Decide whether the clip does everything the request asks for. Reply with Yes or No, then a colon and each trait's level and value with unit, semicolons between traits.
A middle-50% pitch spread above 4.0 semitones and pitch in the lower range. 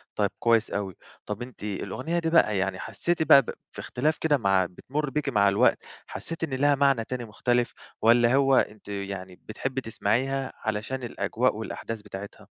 Yes: average, 5.0 semitones; low, 120 Hz